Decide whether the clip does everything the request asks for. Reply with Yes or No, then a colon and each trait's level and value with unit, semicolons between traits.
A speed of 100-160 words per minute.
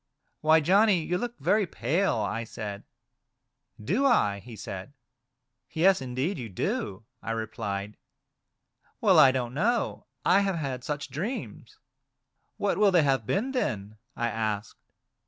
Yes: average, 155 wpm